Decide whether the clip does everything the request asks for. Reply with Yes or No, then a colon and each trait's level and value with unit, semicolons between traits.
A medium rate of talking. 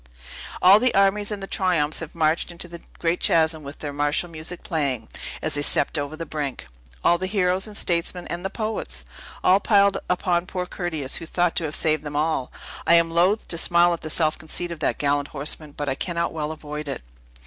No: fast, 210 wpm